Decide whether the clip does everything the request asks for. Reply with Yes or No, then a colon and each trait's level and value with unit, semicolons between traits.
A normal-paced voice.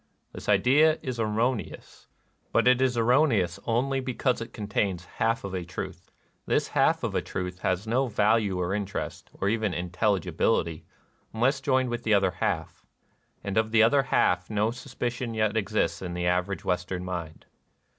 Yes: average, 165 wpm